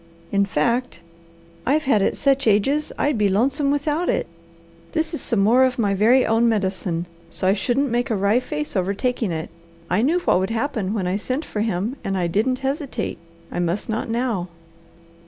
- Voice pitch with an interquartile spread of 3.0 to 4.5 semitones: No, wide, 5.4 semitones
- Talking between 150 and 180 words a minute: No, average, 195 wpm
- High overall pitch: Yes, high, 225 Hz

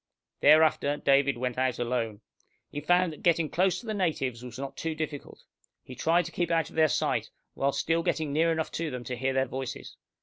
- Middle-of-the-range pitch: Yes, medium, 145 Hz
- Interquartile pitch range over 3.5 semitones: Yes, average, 4.0 semitones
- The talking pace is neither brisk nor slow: No, fast, 210 wpm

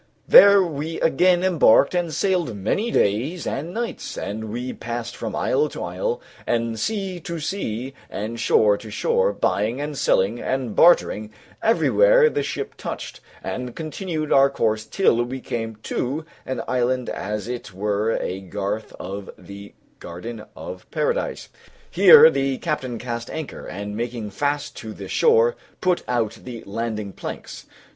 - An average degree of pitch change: No, wide, 8.2 semitones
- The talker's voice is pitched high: No, low, 125 Hz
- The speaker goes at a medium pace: Yes, average, 150 wpm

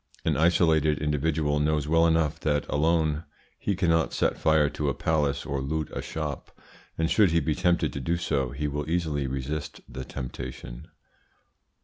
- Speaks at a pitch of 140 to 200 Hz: No, very low, 75 Hz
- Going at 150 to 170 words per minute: Yes, average, 165 wpm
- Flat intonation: Yes, narrow, 2.3 semitones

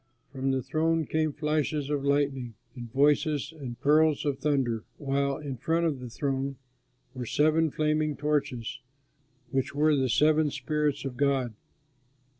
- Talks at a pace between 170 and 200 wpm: No, average, 145 wpm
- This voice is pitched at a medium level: Yes, medium, 145 Hz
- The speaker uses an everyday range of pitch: No, narrow, 2.3 semitones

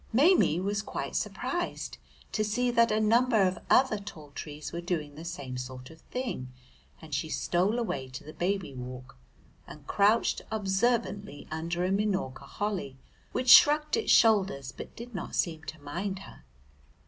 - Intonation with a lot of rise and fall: Yes, wide, 6.5 semitones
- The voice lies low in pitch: No, high, 190 Hz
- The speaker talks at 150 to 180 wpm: Yes, average, 160 wpm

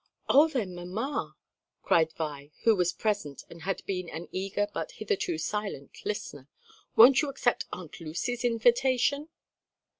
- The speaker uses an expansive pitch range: Yes, wide, 6.7 semitones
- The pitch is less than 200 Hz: No, high, 205 Hz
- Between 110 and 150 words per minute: Yes, average, 140 wpm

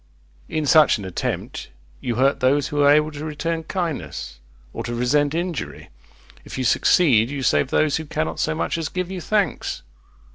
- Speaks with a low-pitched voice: No, medium, 150 Hz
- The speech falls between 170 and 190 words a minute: Yes, average, 180 wpm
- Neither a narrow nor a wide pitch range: Yes, average, 3.5 semitones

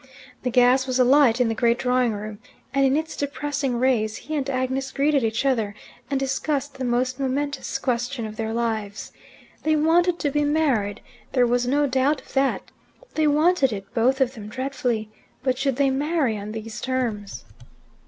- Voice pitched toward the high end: Yes, very high, 260 Hz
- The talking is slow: No, average, 180 wpm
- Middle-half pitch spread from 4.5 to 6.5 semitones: No, average, 3.3 semitones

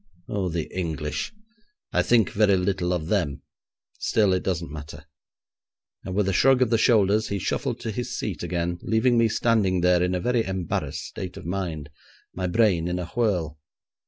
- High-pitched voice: No, very low, 95 Hz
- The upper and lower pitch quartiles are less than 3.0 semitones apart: No, average, 3.8 semitones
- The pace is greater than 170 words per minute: Yes, average, 180 wpm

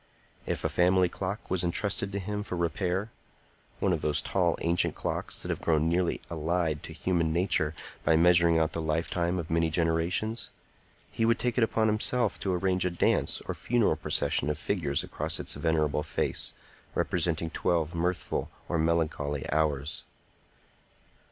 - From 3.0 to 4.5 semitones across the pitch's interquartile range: No, narrow, 2.6 semitones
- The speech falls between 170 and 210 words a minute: No, average, 150 wpm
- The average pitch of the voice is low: Yes, very low, 85 Hz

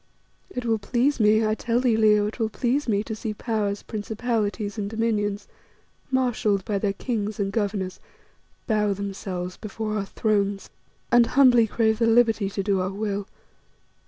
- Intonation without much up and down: Yes, narrow, 2.2 semitones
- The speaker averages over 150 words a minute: Yes, average, 160 wpm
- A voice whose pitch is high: Yes, high, 215 Hz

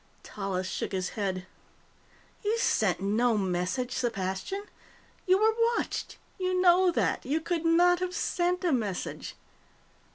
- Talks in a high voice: Yes, very high, 255 Hz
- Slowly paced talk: Yes, slow, 130 wpm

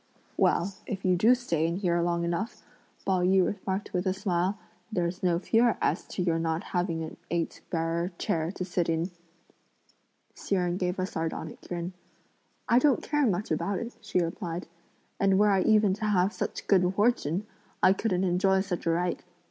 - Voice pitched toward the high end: No, medium, 180 Hz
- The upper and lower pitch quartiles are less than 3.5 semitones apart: Yes, narrow, 2.5 semitones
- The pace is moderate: Yes, average, 180 wpm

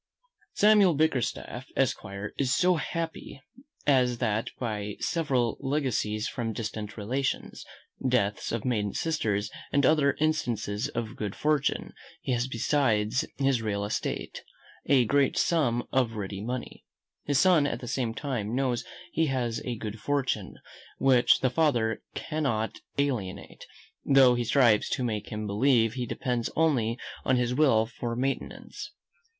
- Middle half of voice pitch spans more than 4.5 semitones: No, average, 4.1 semitones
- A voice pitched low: Yes, low, 125 Hz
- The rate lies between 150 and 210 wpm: No, average, 140 wpm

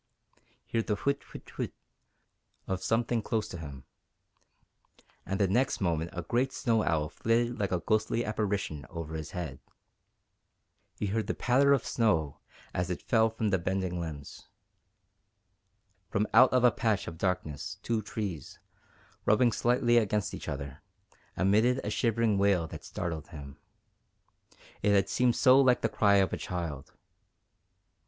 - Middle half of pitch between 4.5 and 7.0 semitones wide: Yes, average, 5.2 semitones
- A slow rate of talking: No, average, 150 wpm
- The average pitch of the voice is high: No, low, 100 Hz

